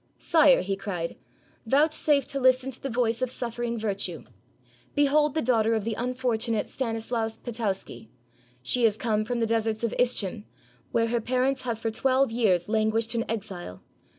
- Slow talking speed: No, average, 170 wpm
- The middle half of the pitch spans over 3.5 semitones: No, average, 2.7 semitones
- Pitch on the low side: No, high, 230 Hz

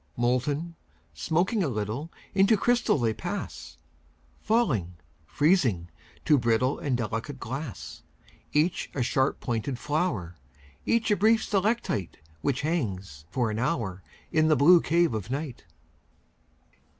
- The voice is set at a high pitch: No, low, 135 Hz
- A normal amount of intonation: No, wide, 7.2 semitones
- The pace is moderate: No, slow, 125 wpm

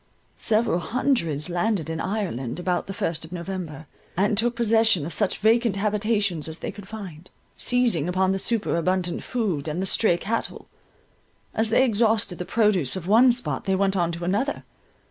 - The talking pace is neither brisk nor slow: Yes, average, 170 wpm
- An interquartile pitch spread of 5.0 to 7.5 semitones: No, average, 4.4 semitones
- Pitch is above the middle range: Yes, high, 195 Hz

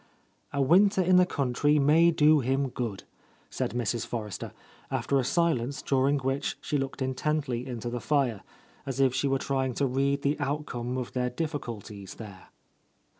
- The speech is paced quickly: No, average, 165 wpm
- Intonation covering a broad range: No, average, 3.0 semitones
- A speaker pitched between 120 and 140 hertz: Yes, low, 135 Hz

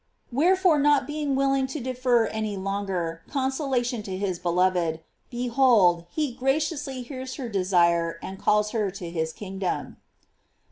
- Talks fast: No, average, 145 wpm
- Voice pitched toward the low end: No, high, 230 Hz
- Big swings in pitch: Yes, wide, 6.3 semitones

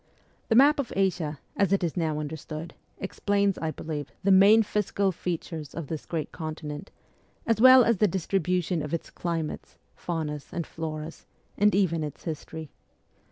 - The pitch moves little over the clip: No, average, 4.1 semitones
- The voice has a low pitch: No, medium, 170 Hz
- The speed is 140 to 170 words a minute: Yes, average, 160 wpm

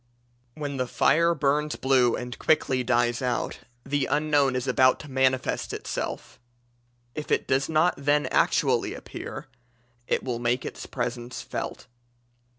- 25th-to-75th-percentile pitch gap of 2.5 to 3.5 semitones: Yes, average, 2.8 semitones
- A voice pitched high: No, low, 130 Hz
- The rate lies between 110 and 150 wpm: Yes, average, 140 wpm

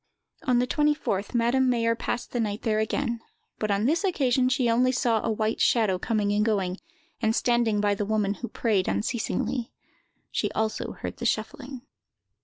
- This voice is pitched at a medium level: No, high, 230 Hz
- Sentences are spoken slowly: No, average, 175 wpm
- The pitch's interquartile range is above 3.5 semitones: No, average, 2.9 semitones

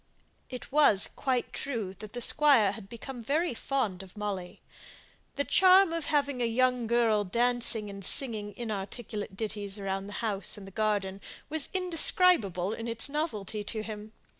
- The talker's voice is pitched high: Yes, high, 225 Hz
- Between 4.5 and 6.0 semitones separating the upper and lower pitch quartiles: Yes, average, 4.9 semitones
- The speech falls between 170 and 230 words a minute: No, average, 155 wpm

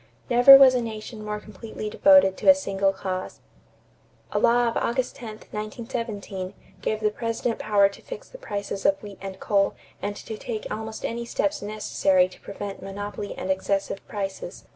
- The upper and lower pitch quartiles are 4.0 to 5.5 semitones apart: No, average, 2.9 semitones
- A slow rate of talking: No, average, 170 wpm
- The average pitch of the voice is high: Yes, high, 210 Hz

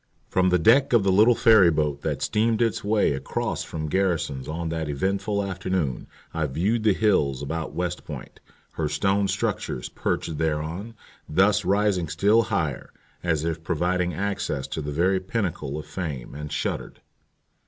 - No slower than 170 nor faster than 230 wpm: No, average, 160 wpm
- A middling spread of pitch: Yes, average, 4.7 semitones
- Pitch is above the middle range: No, very low, 90 Hz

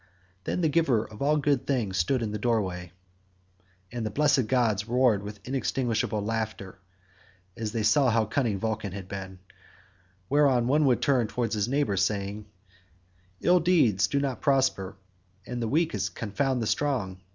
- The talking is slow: No, average, 160 wpm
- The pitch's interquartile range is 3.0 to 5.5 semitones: Yes, average, 4.8 semitones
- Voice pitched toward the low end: Yes, low, 115 Hz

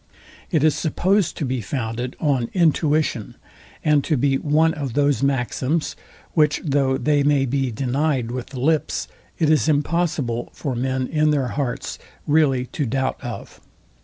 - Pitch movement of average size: Yes, average, 3.0 semitones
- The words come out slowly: No, average, 155 wpm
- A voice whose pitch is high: No, medium, 140 Hz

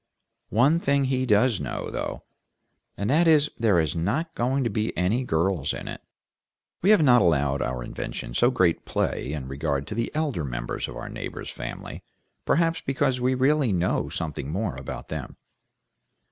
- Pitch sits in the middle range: No, low, 110 Hz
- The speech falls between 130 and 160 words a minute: No, average, 175 wpm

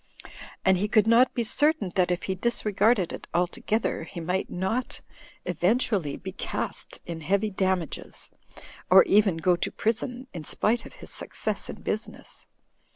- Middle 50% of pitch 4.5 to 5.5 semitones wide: No, average, 4.1 semitones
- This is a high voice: Yes, high, 195 Hz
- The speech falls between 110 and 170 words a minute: Yes, average, 155 wpm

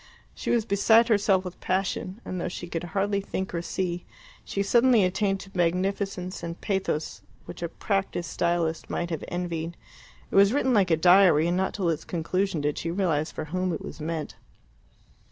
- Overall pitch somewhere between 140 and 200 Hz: Yes, medium, 185 Hz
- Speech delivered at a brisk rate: No, average, 185 wpm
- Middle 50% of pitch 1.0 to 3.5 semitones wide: Yes, average, 2.7 semitones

